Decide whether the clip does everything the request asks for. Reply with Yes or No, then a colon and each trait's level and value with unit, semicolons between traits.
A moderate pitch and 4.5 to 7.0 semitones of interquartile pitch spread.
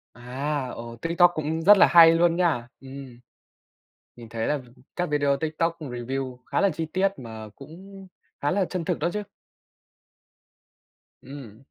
Yes: medium, 150 Hz; average, 5.1 semitones